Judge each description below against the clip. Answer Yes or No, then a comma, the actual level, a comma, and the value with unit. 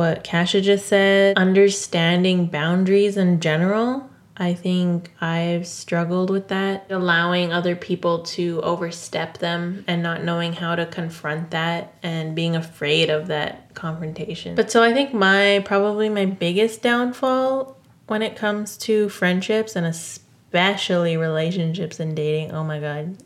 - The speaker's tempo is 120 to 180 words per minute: Yes, average, 140 wpm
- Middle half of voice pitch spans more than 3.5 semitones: No, average, 3.0 semitones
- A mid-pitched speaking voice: Yes, medium, 175 Hz